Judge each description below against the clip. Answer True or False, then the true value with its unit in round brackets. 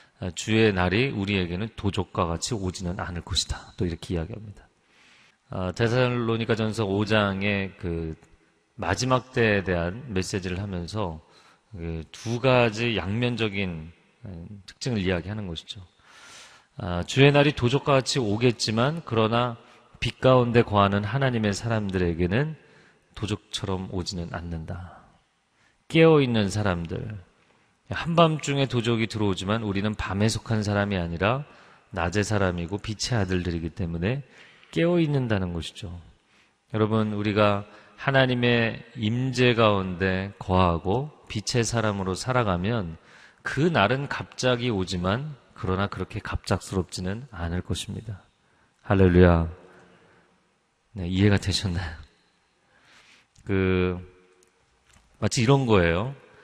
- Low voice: True (105 Hz)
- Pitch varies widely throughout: False (4.5 semitones)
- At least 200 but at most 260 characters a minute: False (270 characters per minute)